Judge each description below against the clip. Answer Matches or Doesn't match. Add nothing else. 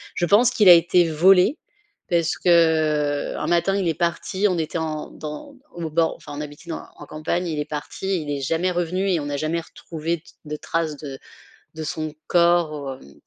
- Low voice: Doesn't match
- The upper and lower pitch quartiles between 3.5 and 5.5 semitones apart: Doesn't match